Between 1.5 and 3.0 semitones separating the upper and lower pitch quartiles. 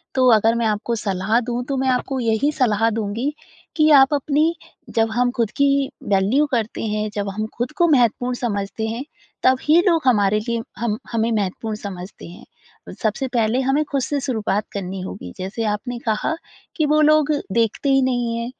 No: average, 3.8 semitones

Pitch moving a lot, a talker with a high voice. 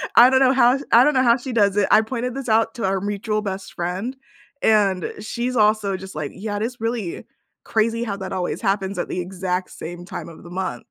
No: average, 3.8 semitones; high, 210 Hz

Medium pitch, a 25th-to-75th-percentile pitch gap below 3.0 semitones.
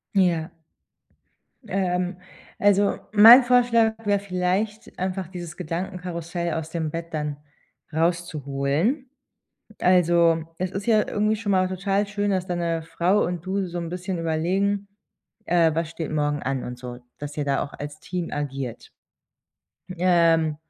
No: medium, 175 Hz; average, 3.5 semitones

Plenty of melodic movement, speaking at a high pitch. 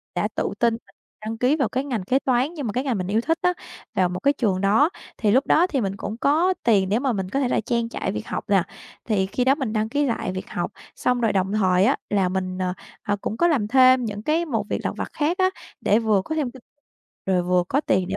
Yes: wide, 5.7 semitones; high, 230 Hz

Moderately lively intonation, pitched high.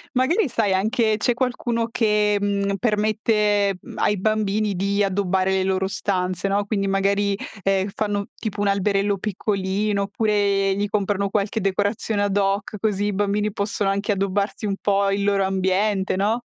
No: narrow, 1.3 semitones; high, 200 Hz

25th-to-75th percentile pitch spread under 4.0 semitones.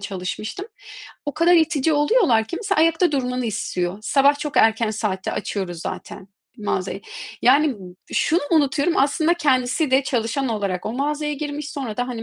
No: wide, 5.5 semitones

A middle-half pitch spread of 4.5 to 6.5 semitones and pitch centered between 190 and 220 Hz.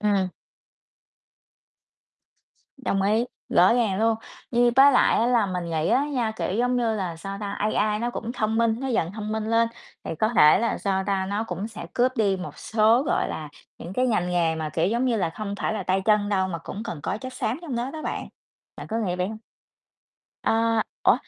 No: average, 3.7 semitones; high, 215 Hz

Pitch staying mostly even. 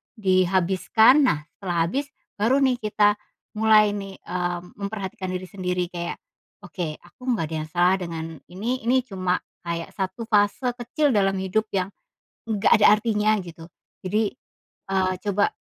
No: average, 3.2 semitones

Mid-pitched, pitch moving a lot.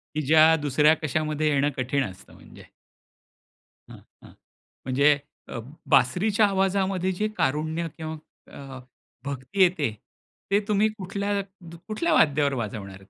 Yes: medium, 155 Hz; wide, 5.8 semitones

